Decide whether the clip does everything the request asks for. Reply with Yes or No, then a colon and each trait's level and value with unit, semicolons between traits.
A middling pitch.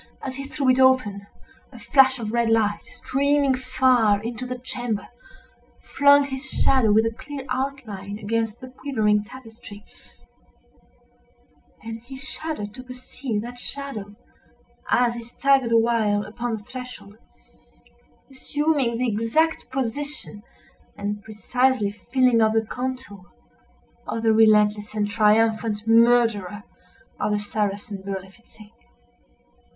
No: high, 230 Hz